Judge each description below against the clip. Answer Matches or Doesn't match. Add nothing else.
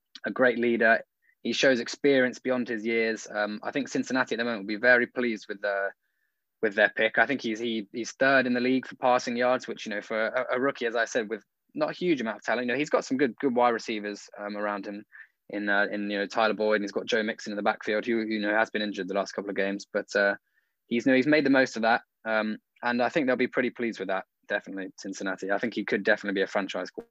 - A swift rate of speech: Matches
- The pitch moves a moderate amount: Matches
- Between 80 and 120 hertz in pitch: Matches